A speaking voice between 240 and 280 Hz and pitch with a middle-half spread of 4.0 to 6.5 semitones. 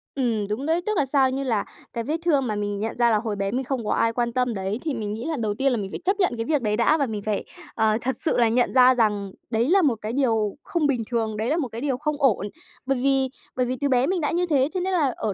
Yes: high, 245 Hz; average, 4.3 semitones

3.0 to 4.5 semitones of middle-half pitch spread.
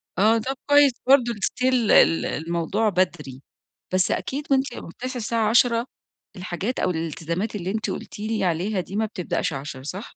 No: wide, 5.5 semitones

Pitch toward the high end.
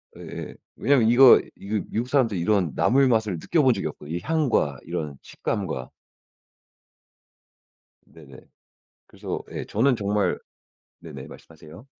No: low, 105 Hz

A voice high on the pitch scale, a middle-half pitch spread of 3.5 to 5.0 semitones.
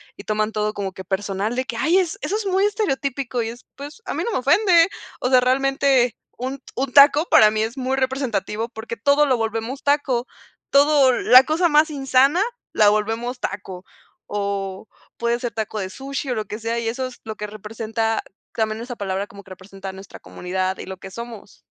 Yes: high, 235 Hz; average, 4.5 semitones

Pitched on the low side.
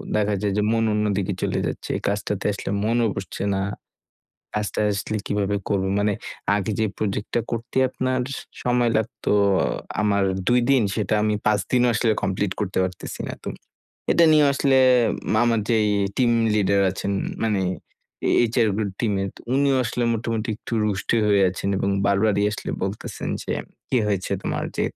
Yes: low, 105 Hz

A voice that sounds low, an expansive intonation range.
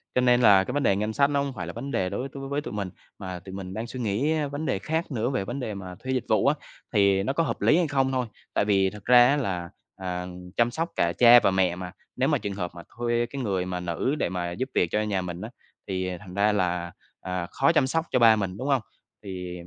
Yes: low, 105 Hz; wide, 6.0 semitones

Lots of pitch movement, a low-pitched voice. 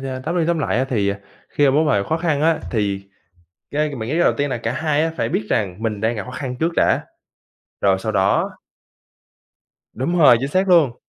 Yes: wide, 6.2 semitones; low, 130 Hz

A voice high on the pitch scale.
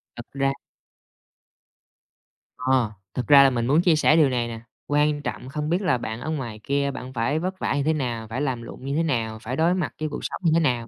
No: medium, 140 Hz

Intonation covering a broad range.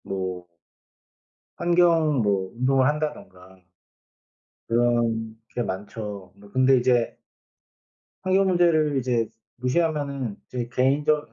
Yes: wide, 5.8 semitones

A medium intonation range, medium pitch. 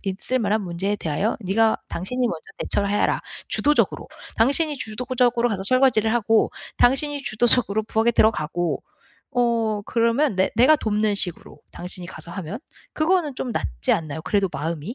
No: average, 4.5 semitones; high, 220 Hz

